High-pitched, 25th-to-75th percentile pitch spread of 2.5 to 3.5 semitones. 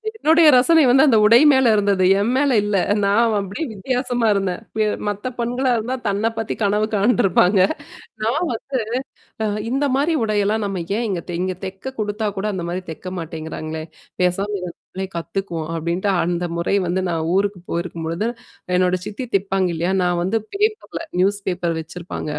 No: high, 200 Hz; average, 4.5 semitones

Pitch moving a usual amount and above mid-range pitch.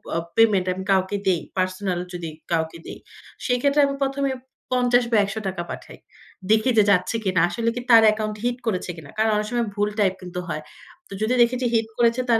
Yes: average, 4.4 semitones; high, 215 Hz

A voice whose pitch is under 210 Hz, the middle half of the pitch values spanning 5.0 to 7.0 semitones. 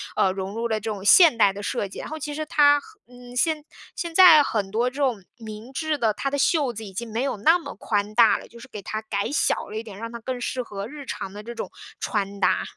No: high, 235 Hz; wide, 5.4 semitones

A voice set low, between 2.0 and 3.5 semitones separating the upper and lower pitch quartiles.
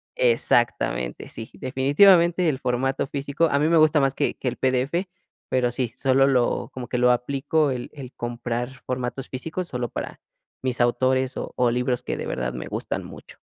Yes: low, 130 Hz; narrow, 2.4 semitones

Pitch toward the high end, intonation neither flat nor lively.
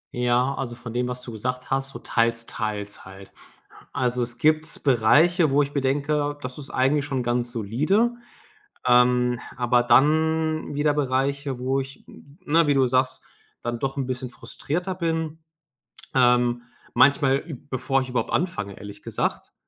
No: low, 130 Hz; average, 3.1 semitones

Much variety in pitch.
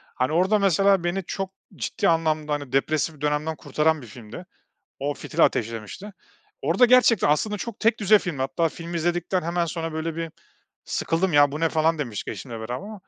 No: average, 4.0 semitones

